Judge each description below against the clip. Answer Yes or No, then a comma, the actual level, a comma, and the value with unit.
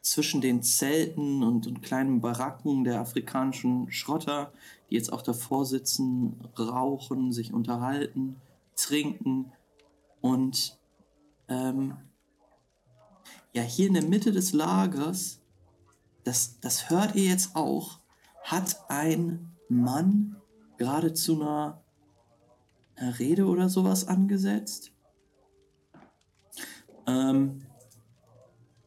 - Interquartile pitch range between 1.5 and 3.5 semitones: No, average, 4.3 semitones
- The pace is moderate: No, slow, 95 wpm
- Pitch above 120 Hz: Yes, low, 135 Hz